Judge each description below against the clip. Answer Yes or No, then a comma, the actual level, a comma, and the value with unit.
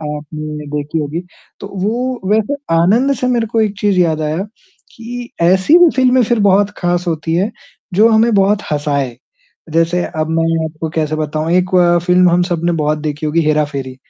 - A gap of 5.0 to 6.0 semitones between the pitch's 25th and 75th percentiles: Yes, wide, 5.4 semitones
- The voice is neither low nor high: Yes, medium, 175 Hz